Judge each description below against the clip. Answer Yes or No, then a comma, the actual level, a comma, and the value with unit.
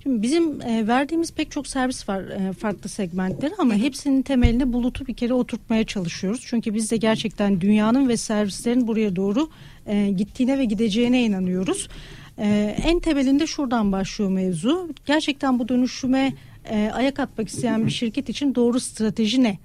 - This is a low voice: No, high, 235 Hz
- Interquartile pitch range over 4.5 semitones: No, average, 4.2 semitones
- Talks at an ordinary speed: No, fast, 145 wpm